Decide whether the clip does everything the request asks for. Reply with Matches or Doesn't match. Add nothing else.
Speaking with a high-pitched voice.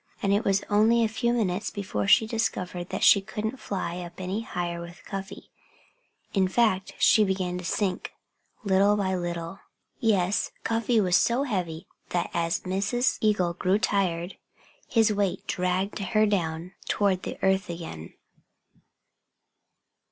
Matches